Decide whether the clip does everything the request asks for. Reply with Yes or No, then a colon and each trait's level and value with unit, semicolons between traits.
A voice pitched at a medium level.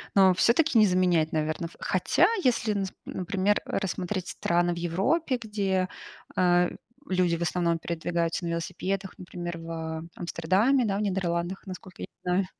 Yes: medium, 180 Hz